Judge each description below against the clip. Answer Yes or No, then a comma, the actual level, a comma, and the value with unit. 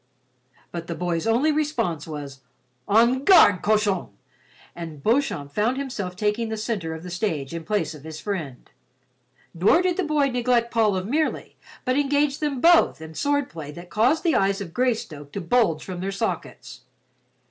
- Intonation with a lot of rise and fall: Yes, wide, 7.3 semitones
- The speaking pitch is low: No, high, 210 Hz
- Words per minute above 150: Yes, average, 170 wpm